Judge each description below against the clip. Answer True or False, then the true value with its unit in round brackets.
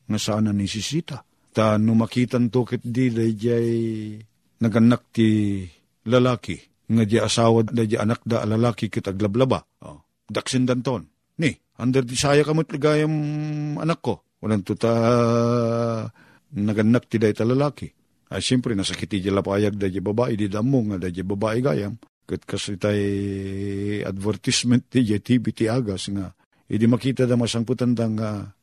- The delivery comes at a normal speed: True (145 wpm)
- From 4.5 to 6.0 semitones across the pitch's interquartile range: False (3.0 semitones)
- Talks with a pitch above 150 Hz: False (115 Hz)